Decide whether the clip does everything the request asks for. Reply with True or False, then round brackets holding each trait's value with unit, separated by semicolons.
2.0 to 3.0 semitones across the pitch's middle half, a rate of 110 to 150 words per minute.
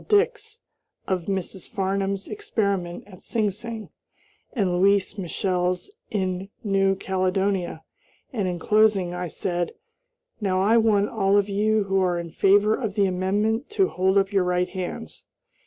True (2.4 semitones; 145 wpm)